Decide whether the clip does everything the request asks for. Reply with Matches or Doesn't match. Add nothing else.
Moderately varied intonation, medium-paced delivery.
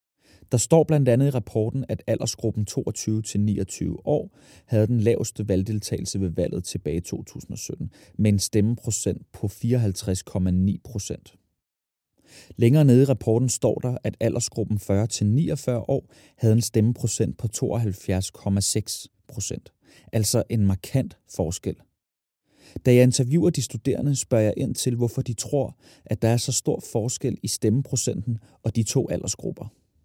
Doesn't match